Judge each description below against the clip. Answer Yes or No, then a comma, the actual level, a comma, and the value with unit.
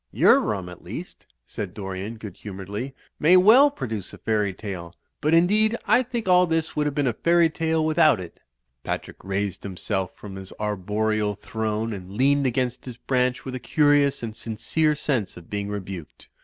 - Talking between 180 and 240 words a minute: Yes, average, 185 wpm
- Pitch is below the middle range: Yes, low, 115 Hz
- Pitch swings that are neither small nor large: No, wide, 7.1 semitones